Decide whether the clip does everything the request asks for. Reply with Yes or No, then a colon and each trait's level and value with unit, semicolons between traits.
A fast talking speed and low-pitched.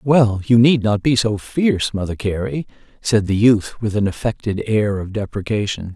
No: average, 180 wpm; low, 110 Hz